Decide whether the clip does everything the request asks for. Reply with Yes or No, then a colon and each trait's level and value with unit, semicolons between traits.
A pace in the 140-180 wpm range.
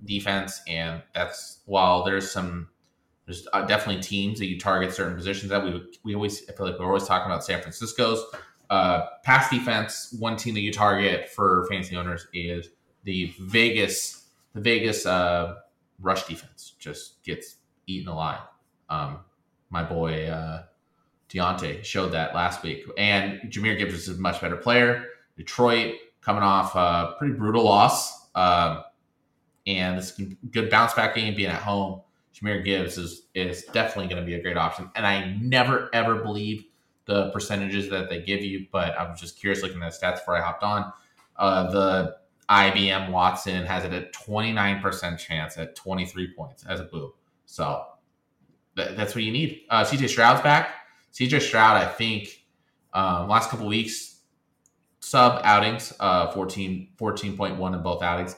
Yes: average, 165 wpm